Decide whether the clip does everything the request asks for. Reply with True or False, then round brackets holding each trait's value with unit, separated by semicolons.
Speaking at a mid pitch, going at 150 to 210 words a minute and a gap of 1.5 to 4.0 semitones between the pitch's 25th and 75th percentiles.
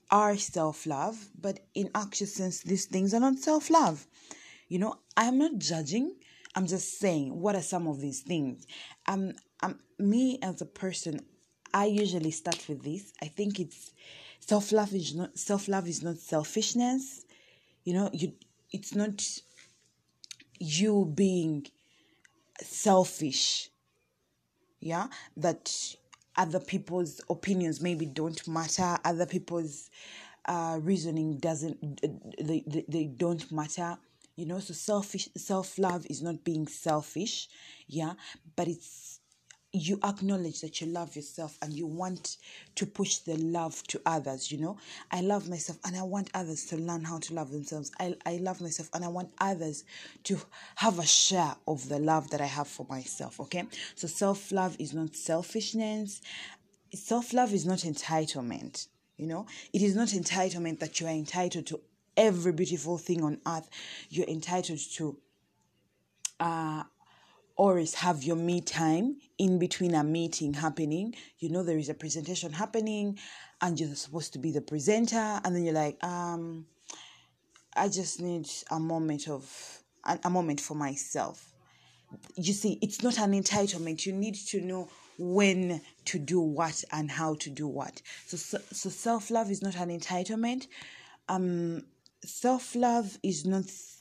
True (175 Hz; 155 wpm; 3.6 semitones)